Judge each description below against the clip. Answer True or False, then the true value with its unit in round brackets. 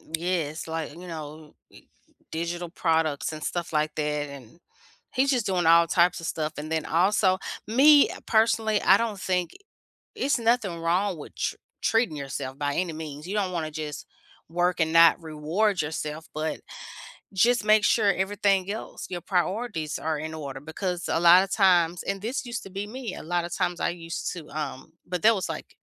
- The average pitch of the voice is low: False (175 Hz)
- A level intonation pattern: False (4.1 semitones)